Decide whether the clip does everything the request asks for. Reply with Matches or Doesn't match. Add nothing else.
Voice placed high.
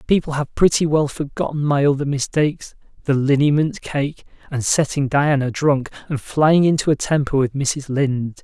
Doesn't match